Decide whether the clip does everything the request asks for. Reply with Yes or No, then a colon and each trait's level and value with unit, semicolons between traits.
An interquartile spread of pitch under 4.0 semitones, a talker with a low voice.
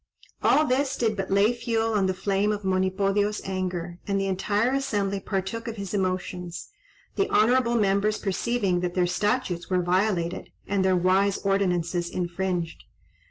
No: narrow, 2.5 semitones; high, 195 Hz